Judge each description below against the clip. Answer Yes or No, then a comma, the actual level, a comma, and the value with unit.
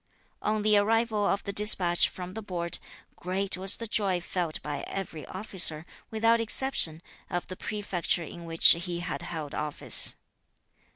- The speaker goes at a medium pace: Yes, average, 155 wpm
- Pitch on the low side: No, medium, 185 Hz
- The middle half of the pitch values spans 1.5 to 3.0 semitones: No, average, 3.6 semitones